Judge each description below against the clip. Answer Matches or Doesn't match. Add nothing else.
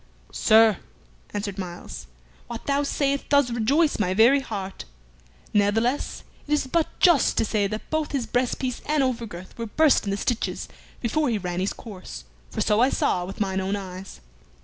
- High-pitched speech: Matches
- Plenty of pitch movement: Matches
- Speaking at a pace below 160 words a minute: Doesn't match